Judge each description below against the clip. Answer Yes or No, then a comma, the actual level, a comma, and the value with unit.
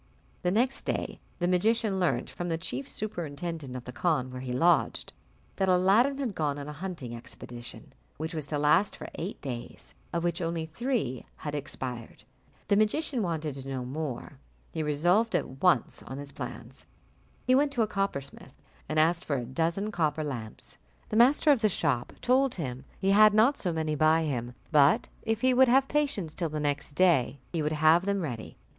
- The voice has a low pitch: No, medium, 165 Hz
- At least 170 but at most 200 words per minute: Yes, average, 190 wpm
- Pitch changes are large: Yes, wide, 6.2 semitones